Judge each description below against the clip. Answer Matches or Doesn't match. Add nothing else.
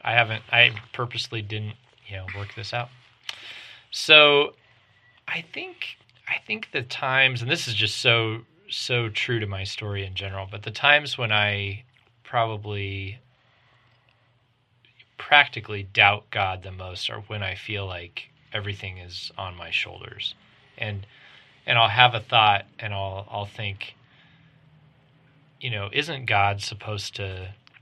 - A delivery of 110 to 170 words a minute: Matches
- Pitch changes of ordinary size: Matches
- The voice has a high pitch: Doesn't match